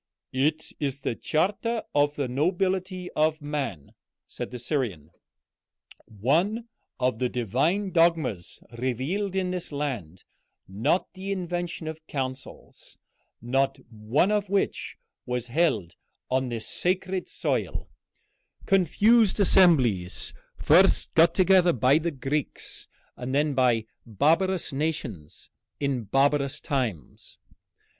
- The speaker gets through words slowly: Yes, slow, 110 wpm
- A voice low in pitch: No, medium, 145 Hz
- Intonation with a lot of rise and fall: Yes, wide, 6.4 semitones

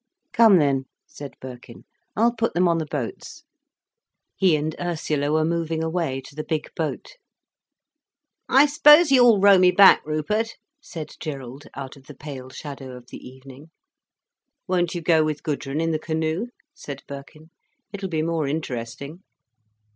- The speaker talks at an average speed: Yes, average, 155 wpm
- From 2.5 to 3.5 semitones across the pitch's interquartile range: No, average, 4.2 semitones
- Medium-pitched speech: Yes, medium, 155 Hz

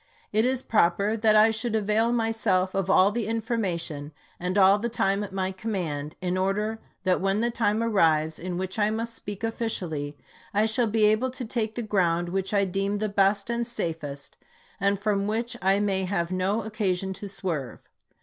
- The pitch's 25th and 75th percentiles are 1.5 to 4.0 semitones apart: Yes, average, 3.1 semitones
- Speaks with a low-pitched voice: No, high, 200 Hz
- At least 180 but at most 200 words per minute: Yes, average, 190 wpm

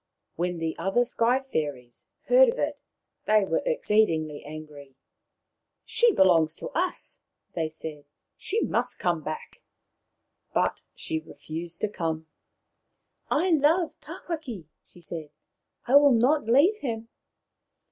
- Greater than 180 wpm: No, slow, 135 wpm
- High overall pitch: Yes, high, 195 Hz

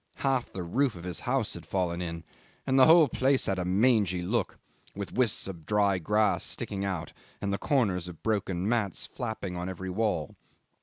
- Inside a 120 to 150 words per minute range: No, average, 190 wpm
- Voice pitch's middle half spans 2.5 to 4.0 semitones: No, average, 4.7 semitones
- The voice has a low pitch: Yes, low, 100 Hz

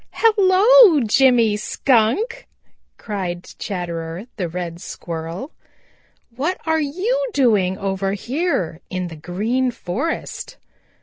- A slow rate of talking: Yes, slow, 100 wpm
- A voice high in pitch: Yes, high, 220 Hz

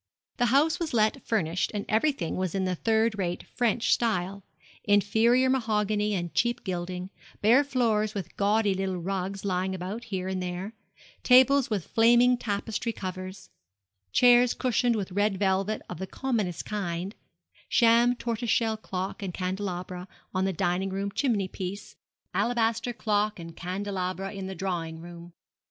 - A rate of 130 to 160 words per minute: Yes, average, 145 wpm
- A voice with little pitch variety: No, average, 3.7 semitones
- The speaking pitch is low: No, high, 200 Hz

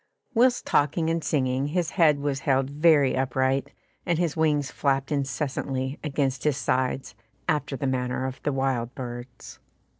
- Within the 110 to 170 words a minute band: Yes, average, 150 wpm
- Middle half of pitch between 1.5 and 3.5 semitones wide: Yes, narrow, 2.4 semitones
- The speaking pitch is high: No, low, 135 Hz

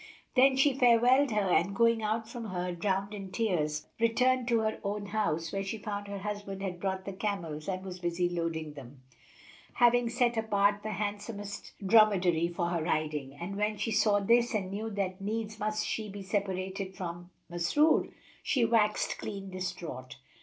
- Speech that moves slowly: No, average, 175 wpm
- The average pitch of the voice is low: No, high, 200 Hz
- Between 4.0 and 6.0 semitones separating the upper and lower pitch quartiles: No, average, 3.4 semitones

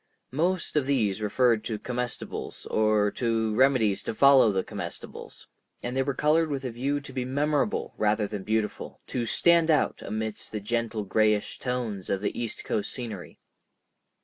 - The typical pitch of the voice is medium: No, low, 115 Hz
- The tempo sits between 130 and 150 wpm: No, average, 165 wpm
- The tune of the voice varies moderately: Yes, average, 4.0 semitones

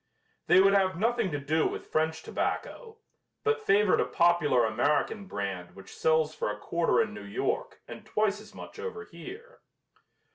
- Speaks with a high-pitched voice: No, medium, 175 Hz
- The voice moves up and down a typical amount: No, wide, 6.7 semitones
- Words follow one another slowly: No, average, 170 wpm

